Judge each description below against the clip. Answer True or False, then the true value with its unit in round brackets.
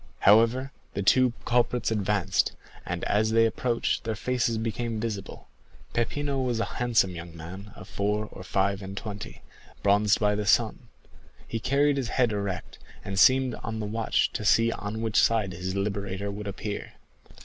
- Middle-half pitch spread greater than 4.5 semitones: False (2.7 semitones)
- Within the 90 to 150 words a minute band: False (165 wpm)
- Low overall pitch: True (105 Hz)